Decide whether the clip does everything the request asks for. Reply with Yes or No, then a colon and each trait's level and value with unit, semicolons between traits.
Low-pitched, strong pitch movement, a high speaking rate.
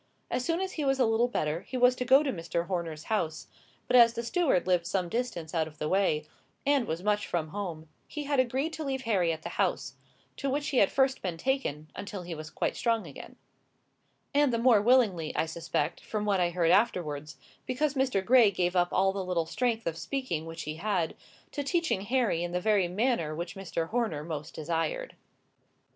No: high, 200 Hz; wide, 7.2 semitones; fast, 210 wpm